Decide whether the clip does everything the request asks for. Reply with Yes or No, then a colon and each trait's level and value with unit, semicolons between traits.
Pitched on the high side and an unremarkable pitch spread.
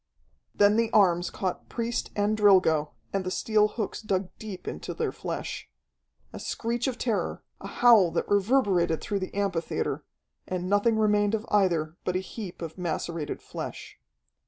Yes: high, 200 Hz; average, 3.2 semitones